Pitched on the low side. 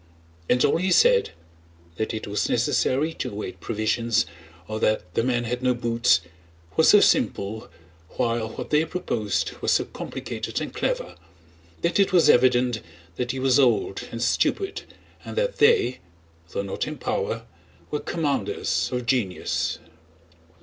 Yes: low, 120 Hz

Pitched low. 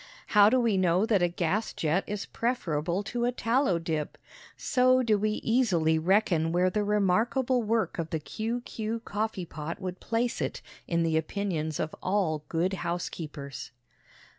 No: high, 190 Hz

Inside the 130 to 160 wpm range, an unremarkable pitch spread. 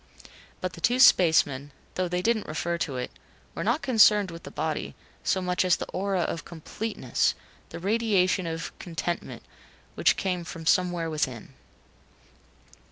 Yes: average, 150 wpm; average, 3.2 semitones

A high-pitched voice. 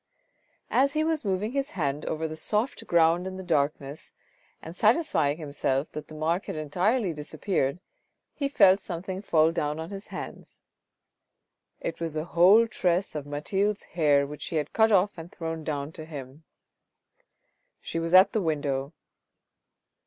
No: medium, 165 Hz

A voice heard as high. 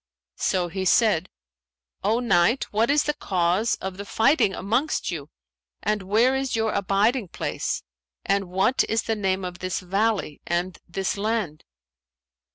Yes: high, 200 Hz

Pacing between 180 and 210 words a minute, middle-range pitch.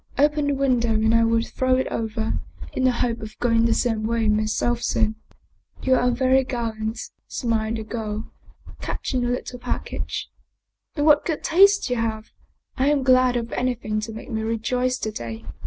No: average, 190 wpm; high, 235 Hz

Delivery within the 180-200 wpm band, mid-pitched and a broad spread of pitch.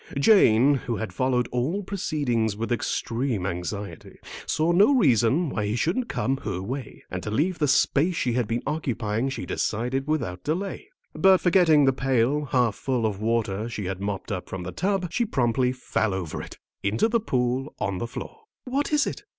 No: average, 185 wpm; low, 125 Hz; wide, 6.2 semitones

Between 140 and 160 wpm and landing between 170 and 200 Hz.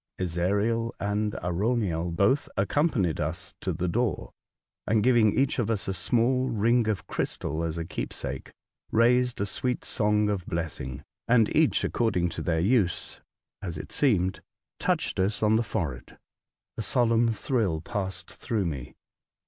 No: average, 150 wpm; low, 105 Hz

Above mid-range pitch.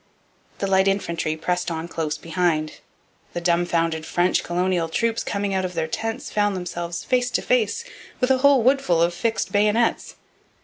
No: medium, 180 Hz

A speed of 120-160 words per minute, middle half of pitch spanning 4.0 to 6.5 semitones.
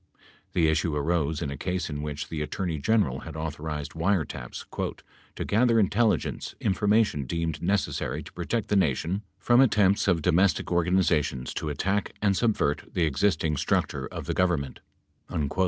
Yes: average, 155 wpm; average, 4.9 semitones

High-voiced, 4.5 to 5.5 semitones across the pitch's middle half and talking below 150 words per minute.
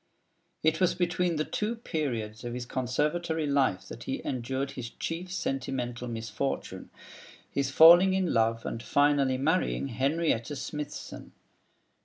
No: medium, 140 Hz; average, 5.0 semitones; slow, 135 wpm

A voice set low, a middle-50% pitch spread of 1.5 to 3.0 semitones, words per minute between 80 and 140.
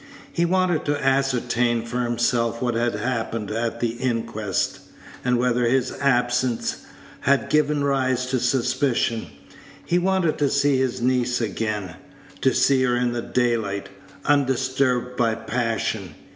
Yes: low, 125 Hz; narrow, 2.4 semitones; slow, 135 wpm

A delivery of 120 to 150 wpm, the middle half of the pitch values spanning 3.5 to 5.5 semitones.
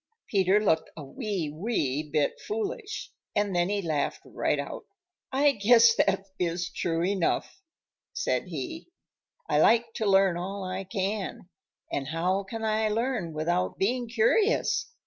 Yes: average, 145 wpm; average, 4.9 semitones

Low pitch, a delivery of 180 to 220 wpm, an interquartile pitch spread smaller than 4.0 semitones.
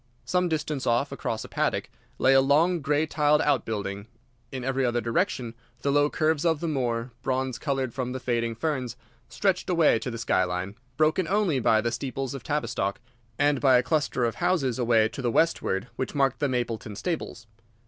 No: low, 130 Hz; average, 190 wpm; average, 4.3 semitones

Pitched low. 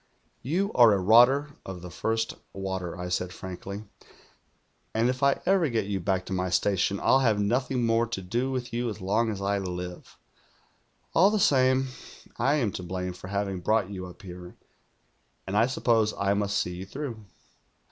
Yes: low, 105 Hz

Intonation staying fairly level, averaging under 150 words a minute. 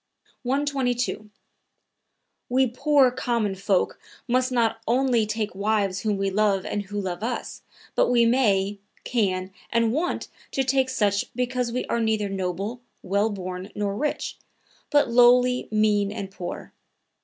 No: average, 3.8 semitones; average, 140 wpm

